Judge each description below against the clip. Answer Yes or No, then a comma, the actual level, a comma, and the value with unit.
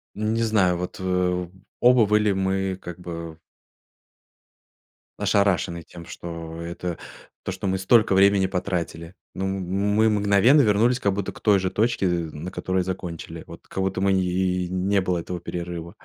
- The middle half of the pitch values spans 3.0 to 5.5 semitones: No, narrow, 2.4 semitones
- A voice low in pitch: Yes, very low, 95 Hz